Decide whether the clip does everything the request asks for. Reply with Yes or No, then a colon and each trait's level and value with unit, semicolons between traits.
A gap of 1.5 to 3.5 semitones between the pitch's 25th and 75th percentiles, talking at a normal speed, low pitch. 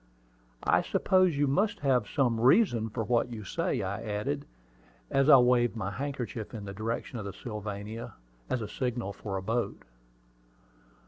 No: average, 4.0 semitones; average, 165 wpm; low, 115 Hz